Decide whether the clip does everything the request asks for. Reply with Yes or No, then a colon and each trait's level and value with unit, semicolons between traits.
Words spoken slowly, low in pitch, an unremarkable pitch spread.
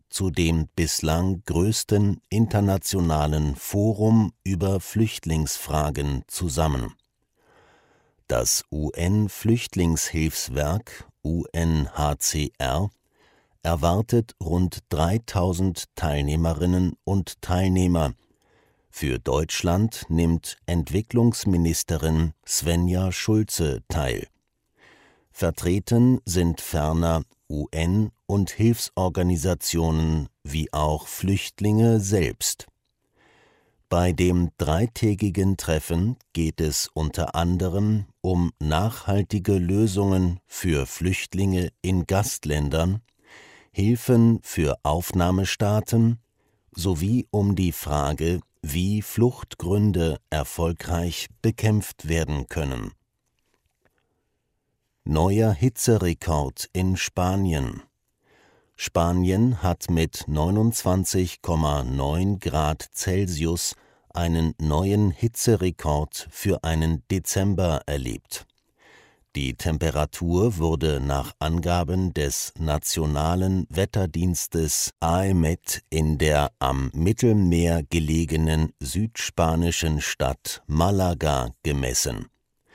Yes: slow, 70 wpm; very low, 85 Hz; average, 3.9 semitones